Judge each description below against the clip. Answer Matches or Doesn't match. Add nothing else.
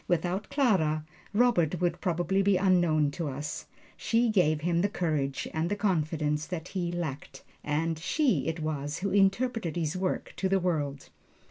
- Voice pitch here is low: Doesn't match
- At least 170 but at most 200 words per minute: Doesn't match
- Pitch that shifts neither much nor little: Matches